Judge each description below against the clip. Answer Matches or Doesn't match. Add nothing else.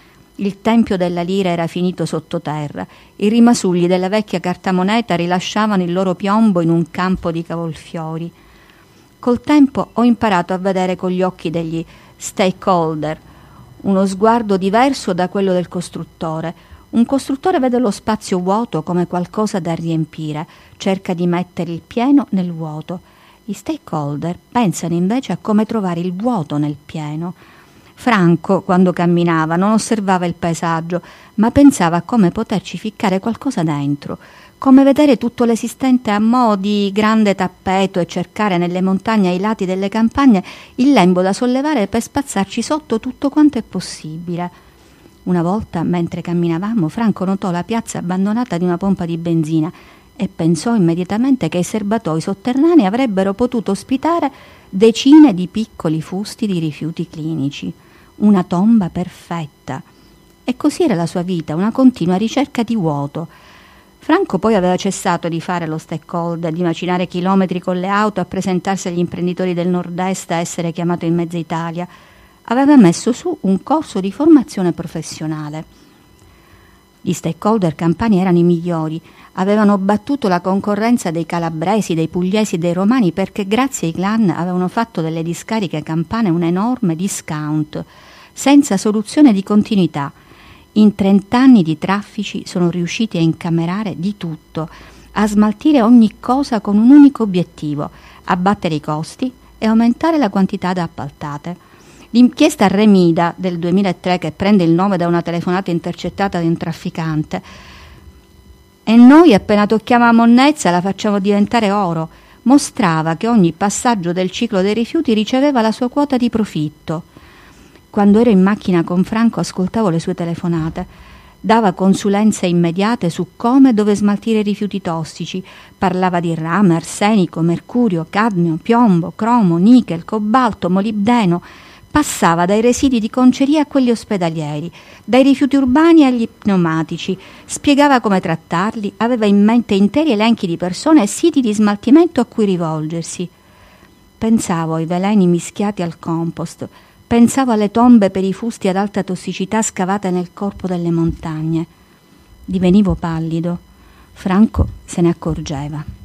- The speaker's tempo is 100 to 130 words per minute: Doesn't match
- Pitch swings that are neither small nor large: Matches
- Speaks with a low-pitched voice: Doesn't match